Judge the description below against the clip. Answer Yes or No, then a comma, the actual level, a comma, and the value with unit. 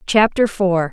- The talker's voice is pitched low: No, high, 190 Hz